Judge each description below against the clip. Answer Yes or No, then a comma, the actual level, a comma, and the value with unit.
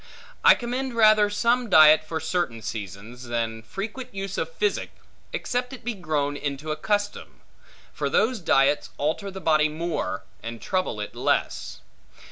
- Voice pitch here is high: No, medium, 160 Hz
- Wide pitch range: Yes, wide, 7.7 semitones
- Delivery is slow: No, average, 150 wpm